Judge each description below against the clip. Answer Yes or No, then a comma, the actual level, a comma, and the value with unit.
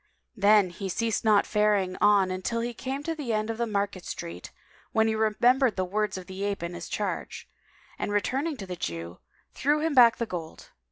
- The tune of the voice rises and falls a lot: No, average, 3.8 semitones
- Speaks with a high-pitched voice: Yes, high, 210 Hz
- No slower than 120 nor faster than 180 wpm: No, fast, 205 wpm